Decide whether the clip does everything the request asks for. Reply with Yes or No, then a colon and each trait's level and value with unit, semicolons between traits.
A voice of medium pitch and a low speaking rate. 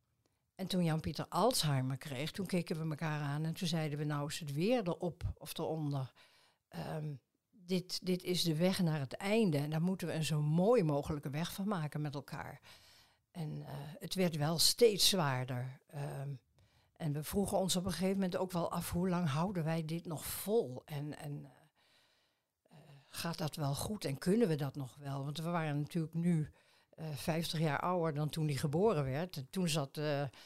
No: medium, 155 Hz; fast, 200 wpm